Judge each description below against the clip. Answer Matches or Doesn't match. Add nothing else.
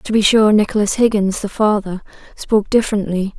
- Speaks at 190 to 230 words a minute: Doesn't match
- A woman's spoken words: Matches